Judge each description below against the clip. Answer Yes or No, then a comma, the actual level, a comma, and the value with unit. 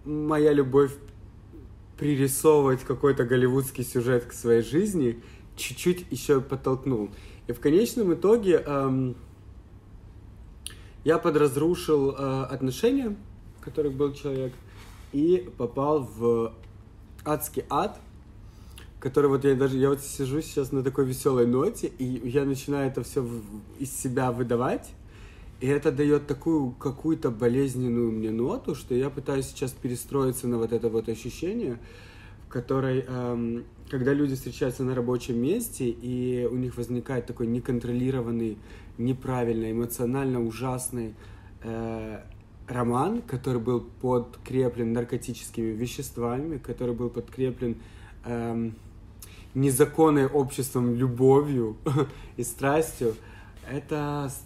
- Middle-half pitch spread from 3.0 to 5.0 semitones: Yes, average, 3.3 semitones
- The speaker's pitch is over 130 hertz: No, low, 125 Hz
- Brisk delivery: No, average, 115 wpm